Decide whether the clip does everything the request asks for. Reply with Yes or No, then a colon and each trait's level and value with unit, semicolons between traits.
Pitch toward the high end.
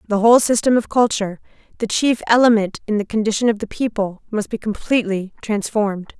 Yes: high, 215 Hz